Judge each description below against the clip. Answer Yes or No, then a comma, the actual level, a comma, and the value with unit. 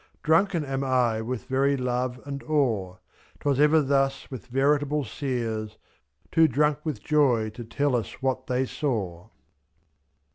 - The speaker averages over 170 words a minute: No, average, 150 wpm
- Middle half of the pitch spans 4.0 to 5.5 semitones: No, average, 3.5 semitones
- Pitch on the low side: Yes, low, 130 Hz